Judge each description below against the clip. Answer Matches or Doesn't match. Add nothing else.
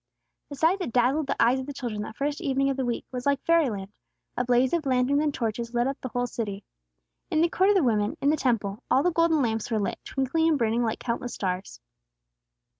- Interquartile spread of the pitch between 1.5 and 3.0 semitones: Doesn't match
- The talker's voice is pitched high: Matches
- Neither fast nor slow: Doesn't match